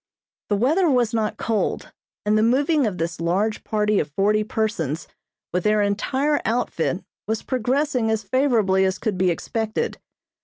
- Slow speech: No, average, 155 wpm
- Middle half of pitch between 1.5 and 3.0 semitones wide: No, average, 4.1 semitones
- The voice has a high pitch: Yes, high, 215 Hz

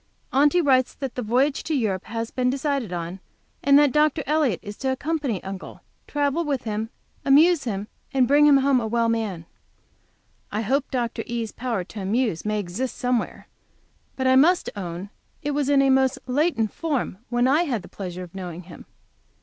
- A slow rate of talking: No, average, 180 wpm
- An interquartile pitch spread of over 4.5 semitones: Yes, average, 5.0 semitones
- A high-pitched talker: Yes, very high, 250 Hz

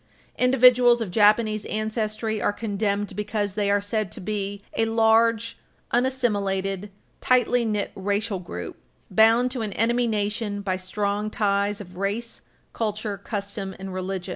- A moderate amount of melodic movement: No, narrow, 2.1 semitones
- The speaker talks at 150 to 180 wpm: No, average, 140 wpm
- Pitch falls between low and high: No, high, 210 Hz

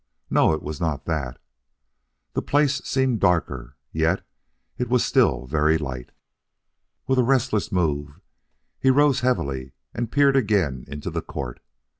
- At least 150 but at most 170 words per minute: No, average, 140 wpm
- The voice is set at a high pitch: No, very low, 85 Hz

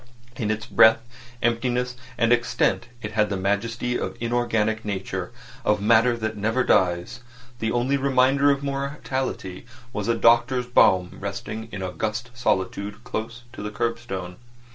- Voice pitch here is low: Yes, low, 115 Hz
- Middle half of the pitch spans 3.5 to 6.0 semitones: No, average, 3.0 semitones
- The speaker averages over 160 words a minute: No, average, 140 wpm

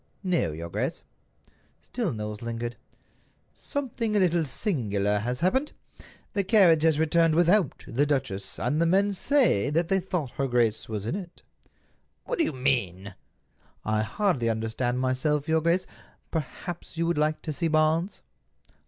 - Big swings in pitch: Yes, wide, 7.1 semitones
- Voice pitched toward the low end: No, medium, 155 Hz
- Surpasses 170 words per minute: No, average, 155 wpm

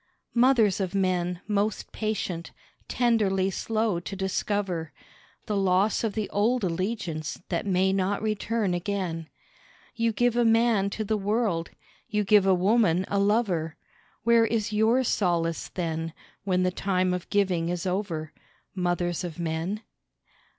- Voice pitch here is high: Yes, high, 195 Hz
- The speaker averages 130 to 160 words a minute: Yes, average, 140 wpm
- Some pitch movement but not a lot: Yes, average, 3.5 semitones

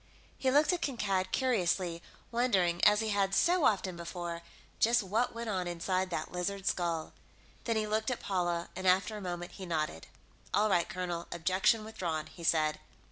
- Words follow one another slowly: No, average, 175 wpm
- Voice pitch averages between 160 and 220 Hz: Yes, medium, 185 Hz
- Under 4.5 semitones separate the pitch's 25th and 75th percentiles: Yes, average, 4.0 semitones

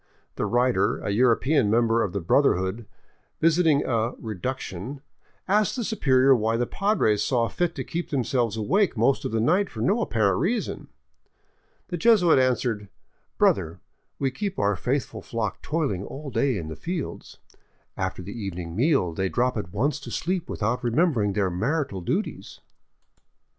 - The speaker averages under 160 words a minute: No, average, 165 wpm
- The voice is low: Yes, low, 120 Hz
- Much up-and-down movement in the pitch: Yes, wide, 6.9 semitones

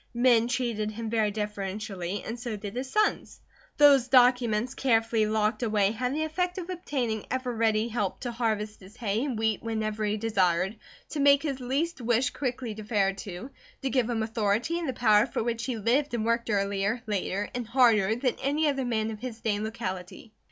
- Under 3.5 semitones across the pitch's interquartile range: Yes, average, 3.1 semitones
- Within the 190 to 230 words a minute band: Yes, average, 195 wpm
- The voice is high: Yes, high, 225 Hz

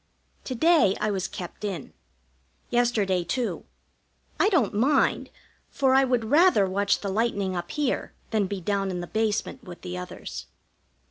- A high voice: Yes, high, 210 Hz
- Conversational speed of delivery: Yes, average, 155 wpm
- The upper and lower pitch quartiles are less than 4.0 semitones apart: No, average, 5.0 semitones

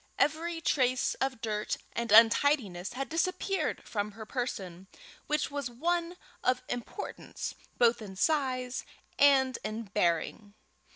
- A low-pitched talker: No, very high, 250 Hz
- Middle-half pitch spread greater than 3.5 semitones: Yes, average, 5.2 semitones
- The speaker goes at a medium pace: No, slow, 120 wpm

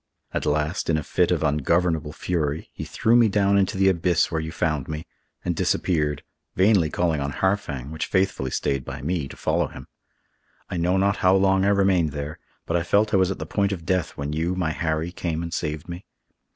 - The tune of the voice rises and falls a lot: No, average, 3.7 semitones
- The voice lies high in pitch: No, very low, 85 Hz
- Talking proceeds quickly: Yes, fast, 215 wpm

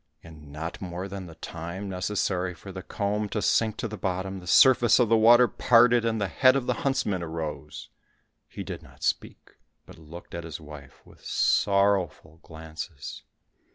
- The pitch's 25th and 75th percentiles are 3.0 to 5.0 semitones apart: Yes, average, 4.5 semitones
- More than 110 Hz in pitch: No, very low, 95 Hz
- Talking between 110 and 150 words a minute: No, average, 175 wpm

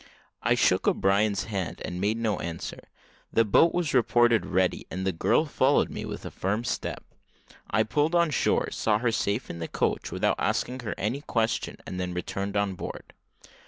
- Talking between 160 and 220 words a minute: Yes, average, 185 wpm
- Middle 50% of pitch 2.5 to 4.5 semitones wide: Yes, average, 4.0 semitones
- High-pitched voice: No, low, 105 Hz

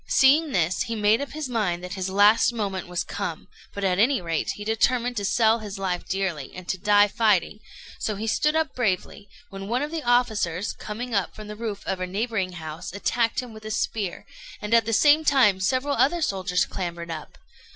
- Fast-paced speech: Yes, fast, 210 wpm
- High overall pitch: Yes, high, 210 Hz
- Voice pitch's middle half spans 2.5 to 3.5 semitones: No, average, 4.2 semitones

